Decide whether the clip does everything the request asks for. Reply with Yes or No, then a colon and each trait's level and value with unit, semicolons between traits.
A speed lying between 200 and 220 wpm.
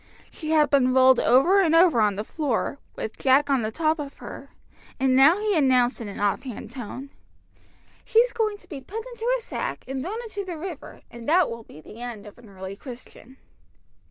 Yes: fast, 205 wpm